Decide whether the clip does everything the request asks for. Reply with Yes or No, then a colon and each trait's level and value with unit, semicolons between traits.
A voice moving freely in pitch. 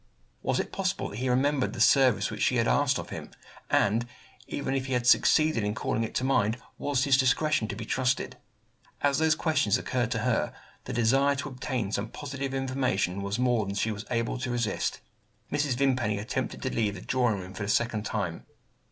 No: average, 4.1 semitones